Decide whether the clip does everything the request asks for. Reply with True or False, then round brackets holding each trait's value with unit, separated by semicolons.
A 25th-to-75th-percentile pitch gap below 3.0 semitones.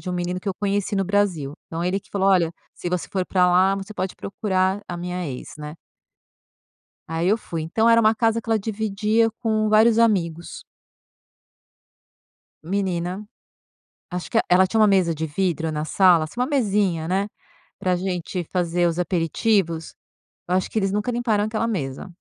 False (3.4 semitones)